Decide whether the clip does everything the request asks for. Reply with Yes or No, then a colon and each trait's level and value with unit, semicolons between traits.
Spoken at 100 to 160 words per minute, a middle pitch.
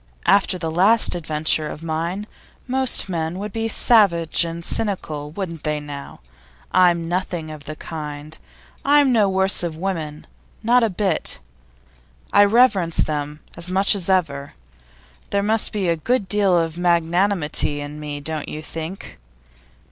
Yes: average, 150 wpm; medium, 170 Hz